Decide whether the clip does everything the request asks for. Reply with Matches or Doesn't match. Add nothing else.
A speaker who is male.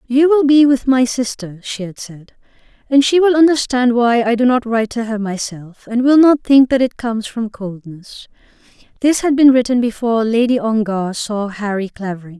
Doesn't match